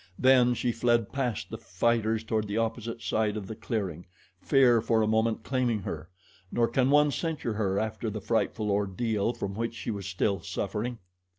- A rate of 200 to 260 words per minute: No, average, 180 wpm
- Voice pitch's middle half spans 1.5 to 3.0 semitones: Yes, narrow, 2.5 semitones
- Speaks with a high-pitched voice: No, low, 110 Hz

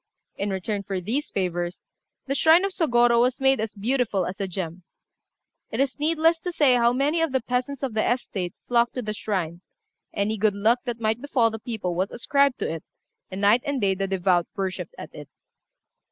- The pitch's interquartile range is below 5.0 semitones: No, wide, 5.4 semitones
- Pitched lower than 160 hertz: No, high, 225 Hz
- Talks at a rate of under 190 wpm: No, average, 200 wpm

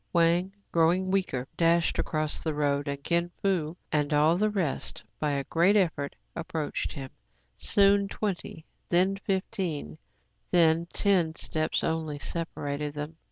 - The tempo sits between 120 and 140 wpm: Yes, slow, 135 wpm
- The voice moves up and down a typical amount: Yes, average, 3.8 semitones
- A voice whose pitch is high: No, medium, 165 Hz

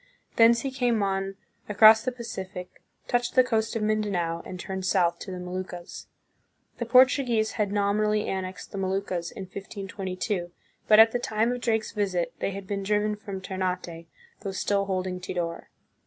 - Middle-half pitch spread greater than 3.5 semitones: No, average, 2.9 semitones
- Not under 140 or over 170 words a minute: Yes, average, 165 wpm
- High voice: Yes, high, 200 Hz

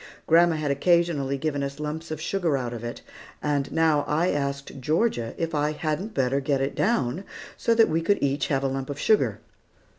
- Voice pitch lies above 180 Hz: No, medium, 150 Hz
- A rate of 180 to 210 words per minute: Yes, average, 200 wpm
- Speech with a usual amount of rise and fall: Yes, average, 3.1 semitones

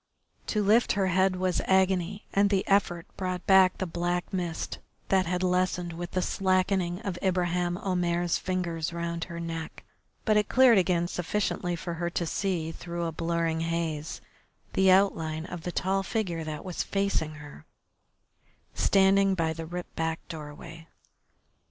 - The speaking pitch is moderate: Yes, medium, 175 Hz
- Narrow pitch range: Yes, narrow, 2.2 semitones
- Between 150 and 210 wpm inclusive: Yes, average, 155 wpm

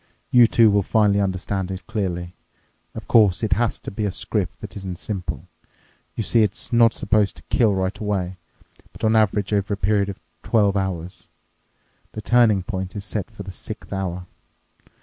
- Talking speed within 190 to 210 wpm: No, average, 180 wpm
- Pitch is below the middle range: Yes, low, 100 Hz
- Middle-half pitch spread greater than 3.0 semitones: No, narrow, 2.4 semitones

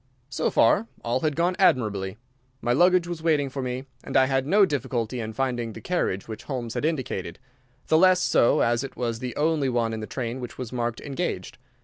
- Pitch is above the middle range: No, low, 130 Hz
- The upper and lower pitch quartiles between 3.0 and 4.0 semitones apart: No, average, 4.8 semitones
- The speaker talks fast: Yes, fast, 210 wpm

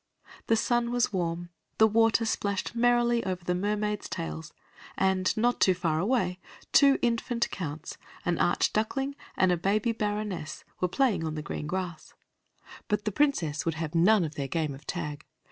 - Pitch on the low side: No, high, 190 Hz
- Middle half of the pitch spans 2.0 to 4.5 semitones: No, average, 5.3 semitones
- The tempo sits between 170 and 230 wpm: No, average, 160 wpm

